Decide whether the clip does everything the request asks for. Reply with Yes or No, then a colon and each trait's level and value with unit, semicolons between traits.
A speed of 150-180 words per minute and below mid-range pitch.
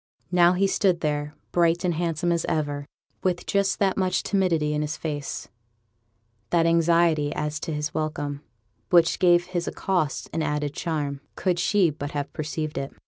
No: average, 165 wpm; medium, 165 Hz